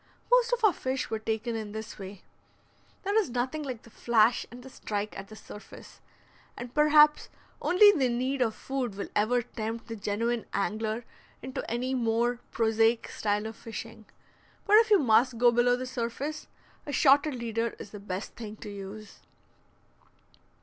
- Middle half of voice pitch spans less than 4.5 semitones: Yes, average, 3.2 semitones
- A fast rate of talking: No, average, 170 wpm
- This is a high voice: Yes, high, 235 Hz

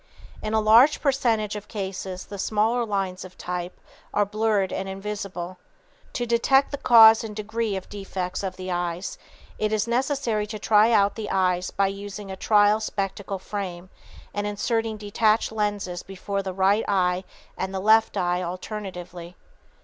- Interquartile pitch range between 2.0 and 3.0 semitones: Yes, narrow, 2.6 semitones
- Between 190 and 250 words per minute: No, average, 160 wpm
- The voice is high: Yes, high, 205 Hz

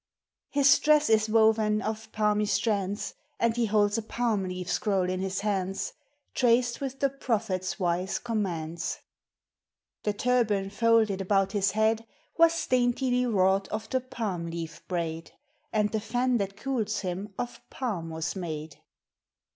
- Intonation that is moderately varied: Yes, average, 3.6 semitones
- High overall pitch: Yes, high, 210 Hz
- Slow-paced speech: No, average, 145 wpm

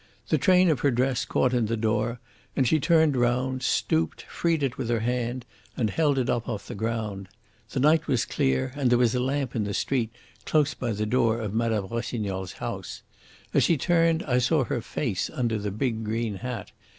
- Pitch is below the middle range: Yes, low, 120 Hz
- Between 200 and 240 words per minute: Yes, fast, 205 wpm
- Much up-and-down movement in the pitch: No, average, 3.5 semitones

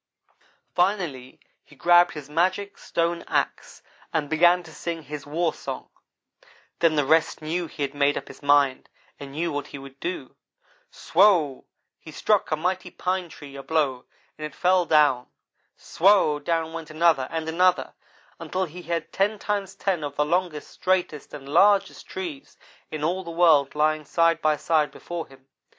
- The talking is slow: No, average, 165 wpm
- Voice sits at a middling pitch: Yes, medium, 160 Hz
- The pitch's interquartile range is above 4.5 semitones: No, average, 3.3 semitones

